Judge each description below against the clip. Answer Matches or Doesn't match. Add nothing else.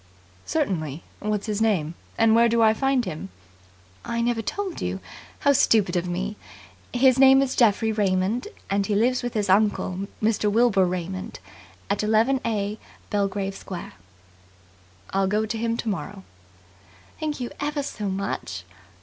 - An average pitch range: Matches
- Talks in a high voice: Matches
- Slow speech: Doesn't match